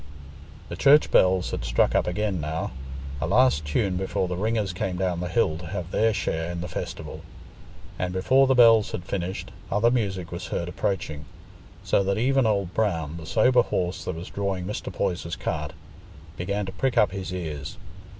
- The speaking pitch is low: Yes, very low, 90 Hz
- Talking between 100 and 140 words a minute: No, average, 180 wpm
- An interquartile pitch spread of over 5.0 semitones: No, average, 3.5 semitones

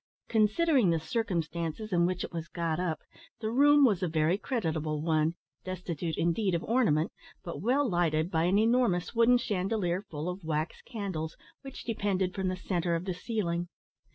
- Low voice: No, medium, 180 Hz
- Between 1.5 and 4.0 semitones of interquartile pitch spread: No, average, 4.8 semitones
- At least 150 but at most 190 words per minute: Yes, average, 170 wpm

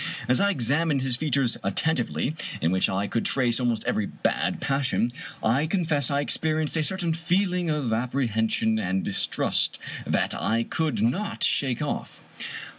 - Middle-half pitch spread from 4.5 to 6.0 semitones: Yes, wide, 5.5 semitones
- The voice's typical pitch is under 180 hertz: Yes, low, 135 Hz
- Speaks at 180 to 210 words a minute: No, average, 150 wpm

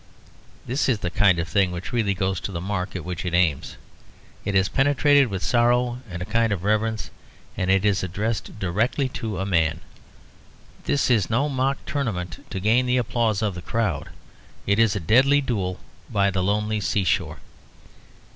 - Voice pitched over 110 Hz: No, low, 105 Hz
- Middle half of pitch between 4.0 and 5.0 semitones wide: Yes, average, 4.3 semitones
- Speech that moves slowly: No, average, 180 wpm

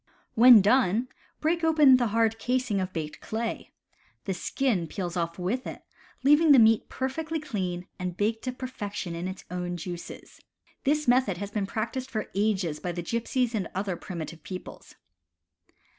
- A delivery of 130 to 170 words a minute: Yes, average, 165 wpm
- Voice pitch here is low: No, high, 215 Hz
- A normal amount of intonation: No, wide, 5.9 semitones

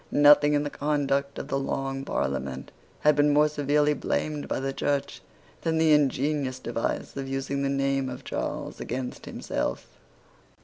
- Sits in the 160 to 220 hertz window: No, medium, 140 Hz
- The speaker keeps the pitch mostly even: Yes, narrow, 1.6 semitones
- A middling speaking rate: Yes, average, 160 wpm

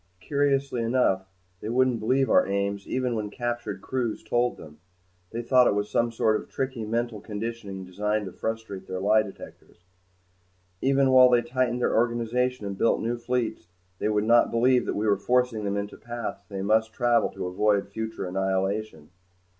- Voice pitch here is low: Yes, low, 110 Hz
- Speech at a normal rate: Yes, average, 180 wpm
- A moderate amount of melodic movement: Yes, average, 3.2 semitones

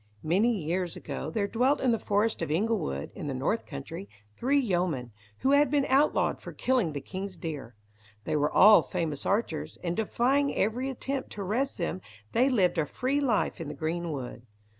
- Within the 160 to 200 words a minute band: Yes, average, 185 wpm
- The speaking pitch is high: Yes, high, 195 Hz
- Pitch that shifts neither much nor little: No, wide, 7.9 semitones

